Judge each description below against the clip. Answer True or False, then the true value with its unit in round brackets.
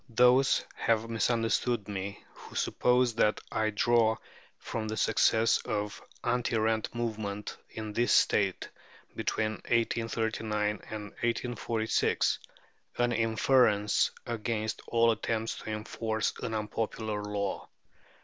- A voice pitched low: True (110 Hz)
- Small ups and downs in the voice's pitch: True (1.7 semitones)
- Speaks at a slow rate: True (110 wpm)